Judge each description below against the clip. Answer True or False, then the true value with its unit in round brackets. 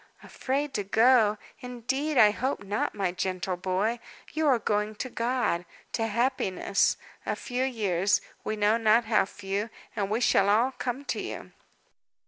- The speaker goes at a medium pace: True (155 wpm)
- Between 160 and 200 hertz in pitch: False (220 Hz)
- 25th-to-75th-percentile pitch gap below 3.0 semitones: False (3.7 semitones)